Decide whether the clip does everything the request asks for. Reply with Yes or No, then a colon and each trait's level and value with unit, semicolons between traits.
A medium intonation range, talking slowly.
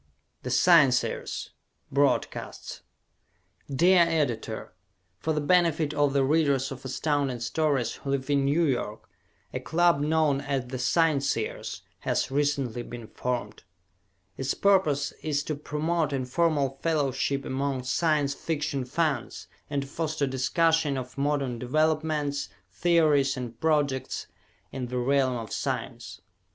Yes: average, 3.0 semitones; slow, 125 wpm